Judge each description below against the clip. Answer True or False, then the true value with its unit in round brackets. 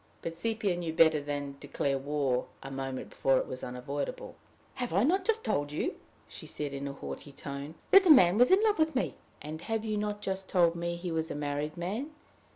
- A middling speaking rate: False (215 wpm)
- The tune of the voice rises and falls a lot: True (6.7 semitones)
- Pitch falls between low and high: True (165 Hz)